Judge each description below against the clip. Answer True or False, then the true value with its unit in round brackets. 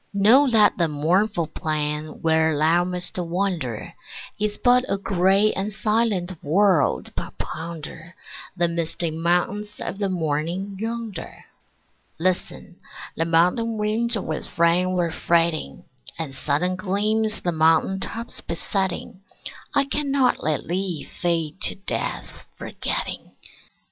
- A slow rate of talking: True (120 wpm)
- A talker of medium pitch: True (180 Hz)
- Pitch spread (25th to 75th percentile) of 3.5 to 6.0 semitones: True (4.2 semitones)